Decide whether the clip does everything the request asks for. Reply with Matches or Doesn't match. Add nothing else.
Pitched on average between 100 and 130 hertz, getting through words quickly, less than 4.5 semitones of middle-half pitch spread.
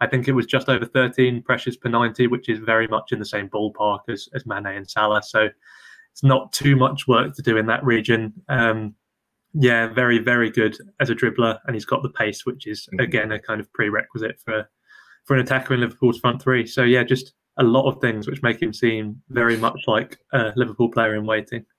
Matches